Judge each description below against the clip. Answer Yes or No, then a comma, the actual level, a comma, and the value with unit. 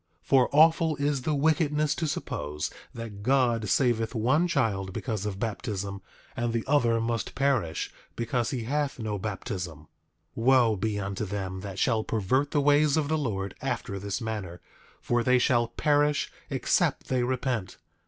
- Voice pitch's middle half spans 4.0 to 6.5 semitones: Yes, wide, 5.4 semitones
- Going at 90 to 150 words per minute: No, average, 165 wpm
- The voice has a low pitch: Yes, low, 120 Hz